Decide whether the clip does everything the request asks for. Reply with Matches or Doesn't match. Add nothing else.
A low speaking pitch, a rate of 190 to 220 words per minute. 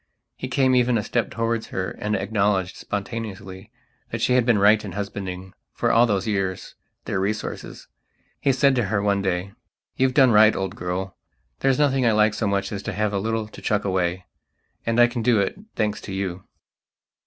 Matches